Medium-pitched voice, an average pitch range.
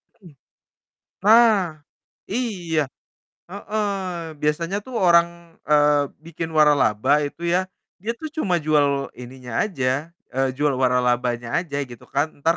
Yes: medium, 160 Hz; average, 4.9 semitones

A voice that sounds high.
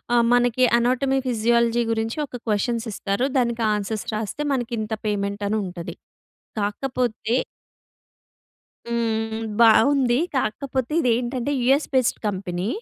Yes: high, 235 Hz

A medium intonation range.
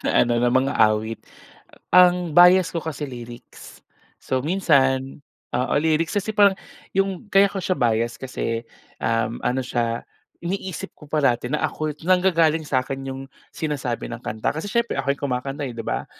No: wide, 6.4 semitones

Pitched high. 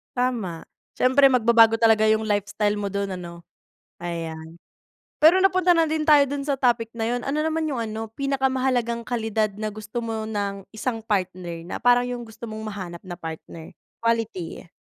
Yes: high, 225 Hz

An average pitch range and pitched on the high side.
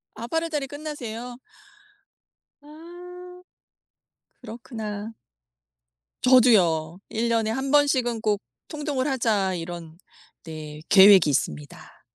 No: wide, 7.1 semitones; high, 235 Hz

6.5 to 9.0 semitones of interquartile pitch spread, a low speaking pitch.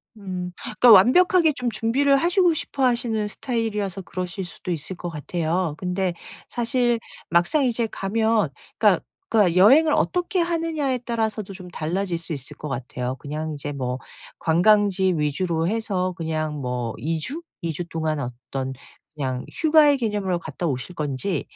No: wide, 7.0 semitones; medium, 185 Hz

